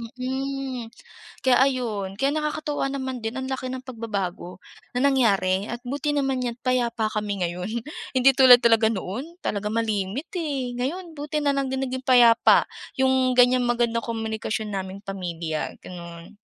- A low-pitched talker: No, high, 245 Hz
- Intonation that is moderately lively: Yes, average, 4.1 semitones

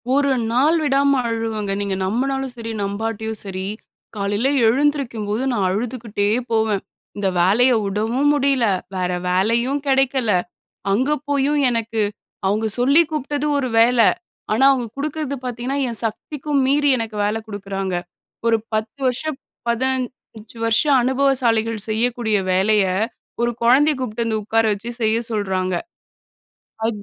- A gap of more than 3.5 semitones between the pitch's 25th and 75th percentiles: Yes, average, 3.9 semitones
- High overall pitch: Yes, high, 230 Hz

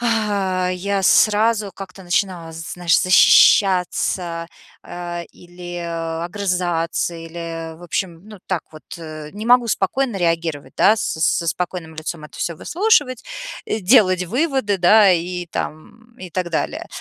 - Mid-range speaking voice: Yes, medium, 180 Hz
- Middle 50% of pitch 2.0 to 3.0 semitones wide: No, average, 3.6 semitones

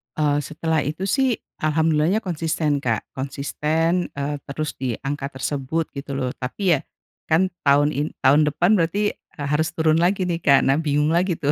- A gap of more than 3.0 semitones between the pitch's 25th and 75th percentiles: No, narrow, 2.5 semitones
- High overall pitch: No, medium, 150 Hz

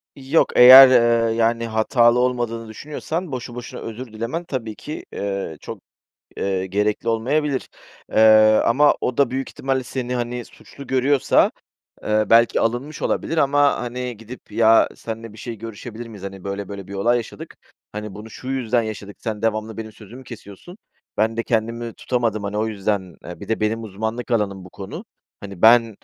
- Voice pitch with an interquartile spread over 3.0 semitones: No, average, 2.7 semitones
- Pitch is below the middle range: Yes, low, 115 Hz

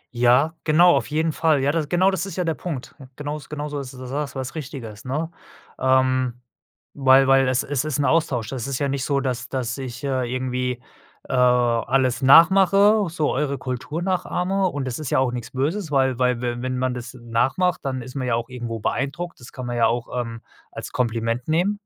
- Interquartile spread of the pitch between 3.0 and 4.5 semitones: Yes, average, 3.6 semitones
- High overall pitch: No, low, 130 Hz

